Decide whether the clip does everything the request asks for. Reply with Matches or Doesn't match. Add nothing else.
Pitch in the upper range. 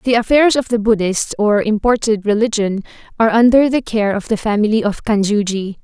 Matches